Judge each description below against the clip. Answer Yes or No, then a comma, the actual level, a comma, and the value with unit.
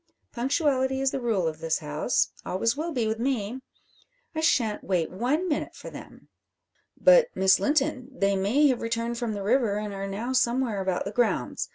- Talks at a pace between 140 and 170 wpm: No, average, 185 wpm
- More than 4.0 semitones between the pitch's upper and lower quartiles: Yes, average, 5.0 semitones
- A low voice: No, high, 235 Hz